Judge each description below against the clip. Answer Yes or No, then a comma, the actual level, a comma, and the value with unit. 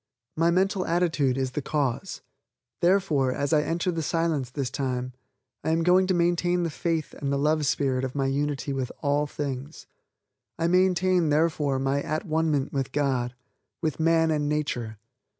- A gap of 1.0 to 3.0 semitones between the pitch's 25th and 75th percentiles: No, average, 3.5 semitones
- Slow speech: No, average, 170 wpm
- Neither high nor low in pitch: Yes, medium, 150 Hz